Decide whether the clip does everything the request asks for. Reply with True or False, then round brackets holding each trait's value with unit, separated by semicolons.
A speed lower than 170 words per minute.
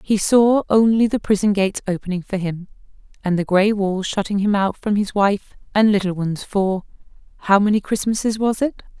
False (180 wpm)